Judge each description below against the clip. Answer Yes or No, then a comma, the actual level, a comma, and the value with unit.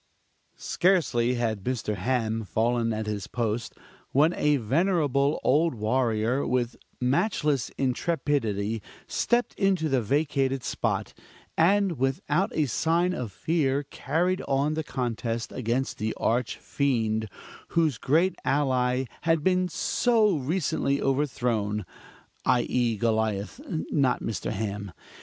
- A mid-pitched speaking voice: No, low, 130 Hz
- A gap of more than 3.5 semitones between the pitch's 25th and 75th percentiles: Yes, average, 5.3 semitones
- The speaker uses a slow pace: Yes, slow, 115 wpm